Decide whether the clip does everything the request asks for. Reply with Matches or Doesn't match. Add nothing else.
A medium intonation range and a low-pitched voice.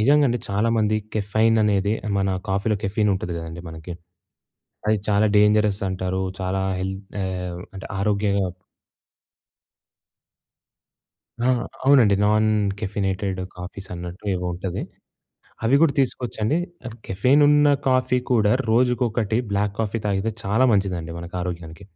Matches